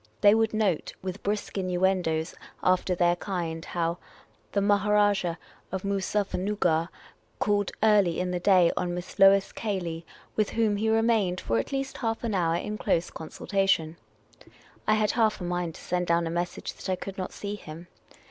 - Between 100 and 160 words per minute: No, average, 175 wpm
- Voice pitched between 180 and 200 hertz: Yes, high, 190 Hz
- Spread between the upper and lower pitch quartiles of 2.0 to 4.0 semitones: Yes, average, 3.0 semitones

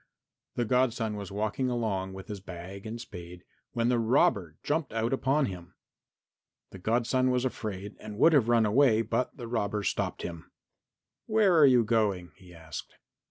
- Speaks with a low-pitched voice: Yes, low, 110 Hz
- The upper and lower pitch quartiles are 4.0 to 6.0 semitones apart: Yes, average, 4.5 semitones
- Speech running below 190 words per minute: Yes, average, 165 wpm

